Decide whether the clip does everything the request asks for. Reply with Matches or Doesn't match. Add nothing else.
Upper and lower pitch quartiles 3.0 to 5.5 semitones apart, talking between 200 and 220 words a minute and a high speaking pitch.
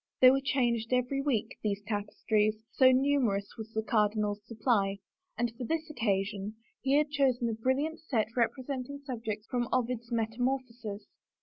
Doesn't match